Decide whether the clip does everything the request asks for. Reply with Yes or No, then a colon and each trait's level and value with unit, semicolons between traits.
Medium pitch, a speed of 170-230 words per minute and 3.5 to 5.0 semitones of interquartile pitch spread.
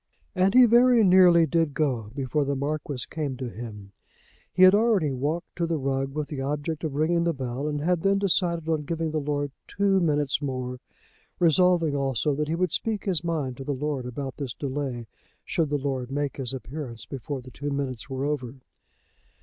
Yes: medium, 145 Hz; average, 195 wpm; average, 3.9 semitones